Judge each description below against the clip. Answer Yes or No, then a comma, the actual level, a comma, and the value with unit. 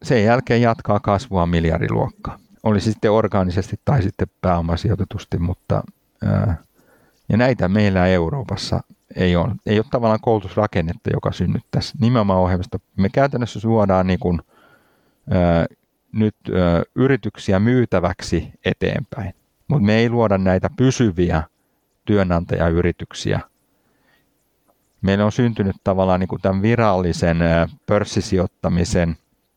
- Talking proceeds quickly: No, average, 110 wpm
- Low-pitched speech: Yes, low, 100 Hz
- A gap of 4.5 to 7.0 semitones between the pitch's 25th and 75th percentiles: No, average, 3.5 semitones